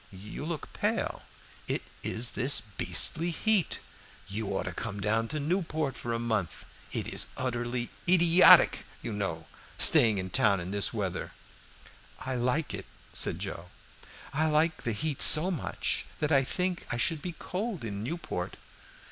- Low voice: Yes, low, 125 Hz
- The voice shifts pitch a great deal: Yes, wide, 7.4 semitones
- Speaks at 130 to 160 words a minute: Yes, average, 155 wpm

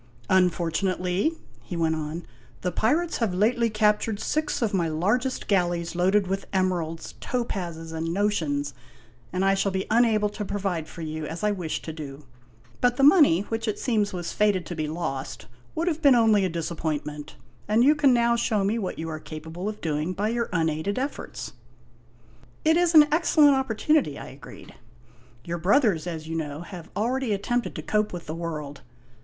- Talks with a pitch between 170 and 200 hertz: Yes, medium, 185 Hz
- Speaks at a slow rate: No, average, 185 wpm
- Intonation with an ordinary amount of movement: No, wide, 5.8 semitones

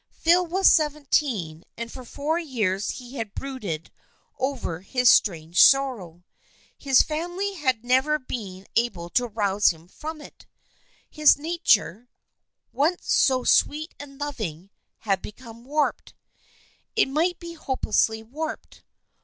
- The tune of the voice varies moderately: No, wide, 6.6 semitones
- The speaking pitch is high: Yes, very high, 255 Hz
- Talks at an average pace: No, slow, 130 wpm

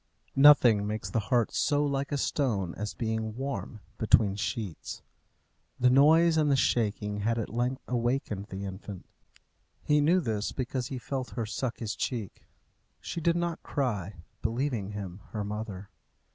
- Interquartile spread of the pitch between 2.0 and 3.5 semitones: No, average, 4.7 semitones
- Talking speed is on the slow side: No, average, 155 wpm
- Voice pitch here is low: Yes, low, 115 Hz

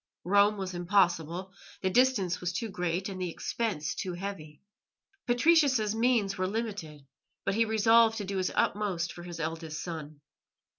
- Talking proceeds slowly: No, average, 155 wpm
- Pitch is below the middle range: No, high, 190 Hz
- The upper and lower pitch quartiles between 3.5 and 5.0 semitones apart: Yes, average, 4.1 semitones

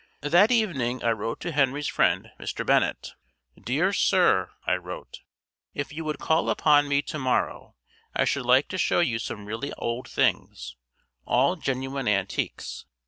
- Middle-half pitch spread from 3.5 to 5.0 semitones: Yes, average, 4.3 semitones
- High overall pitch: No, low, 135 Hz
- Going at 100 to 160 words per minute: Yes, average, 155 wpm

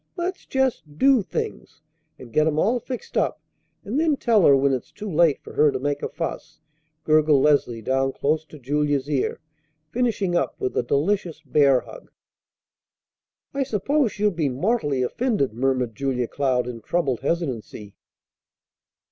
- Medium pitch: Yes, medium, 150 Hz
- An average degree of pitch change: No, wide, 7.6 semitones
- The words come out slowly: No, average, 155 wpm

